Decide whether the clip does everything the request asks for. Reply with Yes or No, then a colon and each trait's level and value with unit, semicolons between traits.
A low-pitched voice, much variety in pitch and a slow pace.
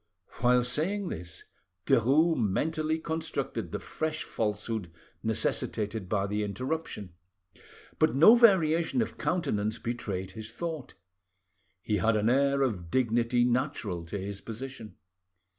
Yes: low, 120 Hz; wide, 6.9 semitones; slow, 120 wpm